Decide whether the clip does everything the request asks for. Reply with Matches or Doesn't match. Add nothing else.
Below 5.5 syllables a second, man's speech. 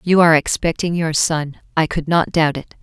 Doesn't match